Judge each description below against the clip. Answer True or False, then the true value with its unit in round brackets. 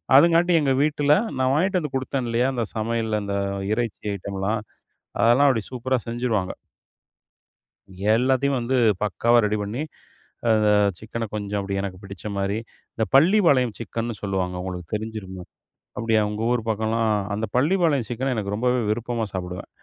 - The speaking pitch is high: False (115 Hz)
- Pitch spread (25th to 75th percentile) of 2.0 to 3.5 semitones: False (4.0 semitones)